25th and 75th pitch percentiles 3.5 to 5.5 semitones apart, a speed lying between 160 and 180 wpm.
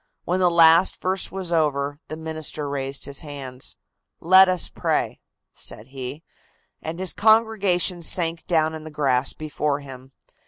No: average, 4.1 semitones; average, 150 wpm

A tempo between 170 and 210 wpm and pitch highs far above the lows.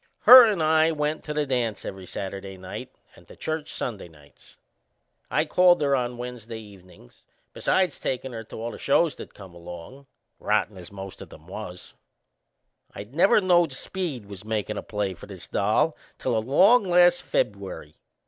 Yes: average, 175 wpm; wide, 8.2 semitones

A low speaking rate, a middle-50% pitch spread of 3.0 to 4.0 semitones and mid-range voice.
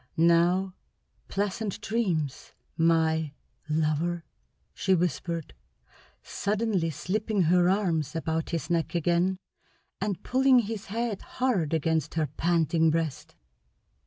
Yes: slow, 100 wpm; average, 3.6 semitones; medium, 170 Hz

